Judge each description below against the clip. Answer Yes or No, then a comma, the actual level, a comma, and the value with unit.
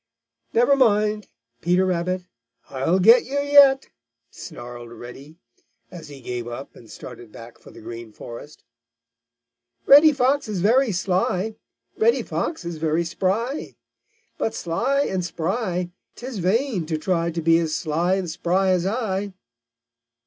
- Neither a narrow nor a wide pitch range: No, wide, 6.2 semitones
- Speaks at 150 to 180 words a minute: No, average, 140 wpm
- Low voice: No, medium, 185 Hz